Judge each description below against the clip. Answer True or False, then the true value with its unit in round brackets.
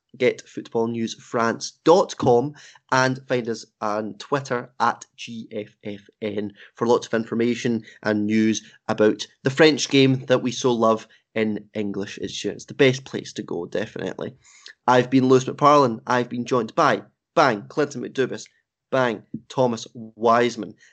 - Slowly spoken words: True (130 wpm)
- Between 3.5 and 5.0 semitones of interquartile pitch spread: False (2.8 semitones)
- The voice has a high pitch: False (115 Hz)